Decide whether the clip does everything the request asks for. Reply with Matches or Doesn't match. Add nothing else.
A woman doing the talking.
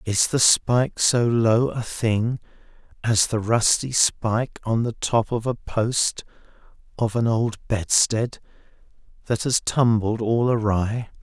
Doesn't match